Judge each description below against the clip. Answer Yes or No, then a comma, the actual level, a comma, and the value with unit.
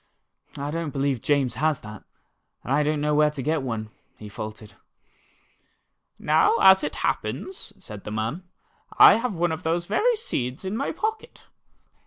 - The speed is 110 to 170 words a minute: Yes, average, 165 wpm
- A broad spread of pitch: Yes, wide, 6.5 semitones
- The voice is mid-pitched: Yes, medium, 150 Hz